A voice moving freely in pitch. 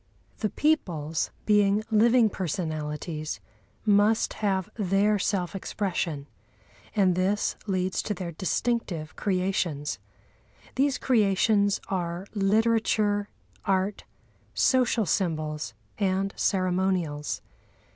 No: average, 3.3 semitones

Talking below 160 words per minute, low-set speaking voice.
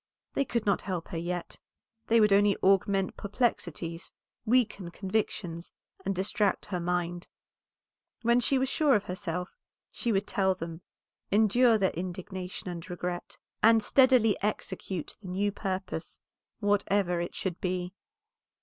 No: slow, 135 wpm; high, 195 Hz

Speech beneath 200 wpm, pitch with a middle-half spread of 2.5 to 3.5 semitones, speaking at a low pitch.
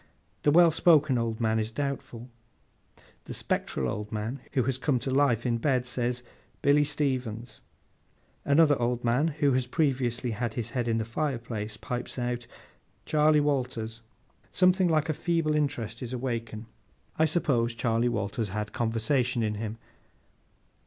No: average, 150 wpm; average, 4.0 semitones; low, 125 Hz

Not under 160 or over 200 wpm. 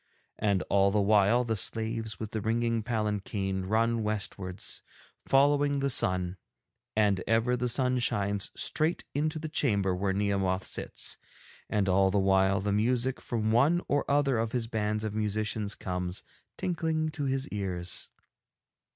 No: average, 150 wpm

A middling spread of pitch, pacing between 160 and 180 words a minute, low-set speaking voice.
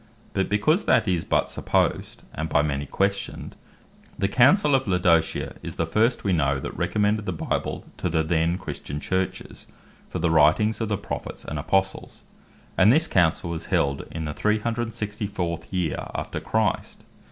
Yes: average, 4.8 semitones; average, 165 wpm; very low, 95 Hz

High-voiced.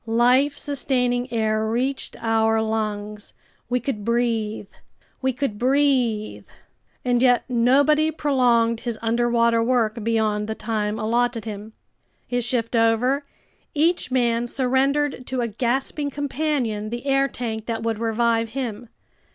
Yes: high, 235 Hz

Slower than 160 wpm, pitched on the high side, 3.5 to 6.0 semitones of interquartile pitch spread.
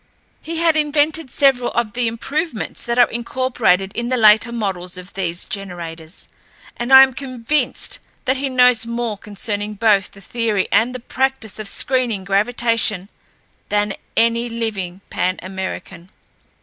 Yes: average, 145 wpm; high, 230 Hz; average, 4.3 semitones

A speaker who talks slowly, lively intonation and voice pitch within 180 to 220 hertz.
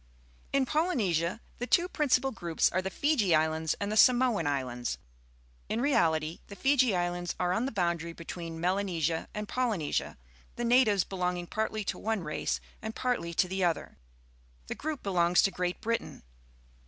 No: average, 165 wpm; wide, 5.9 semitones; high, 190 Hz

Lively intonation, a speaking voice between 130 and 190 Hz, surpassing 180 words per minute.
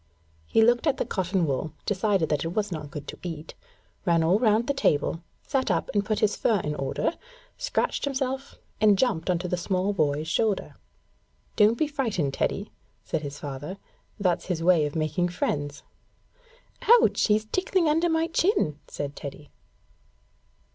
No: wide, 6.9 semitones; medium, 185 Hz; average, 165 wpm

